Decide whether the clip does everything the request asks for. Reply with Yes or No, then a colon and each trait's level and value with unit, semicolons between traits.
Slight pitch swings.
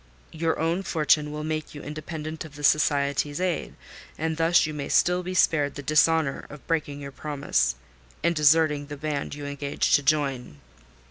Yes: narrow, 2.0 semitones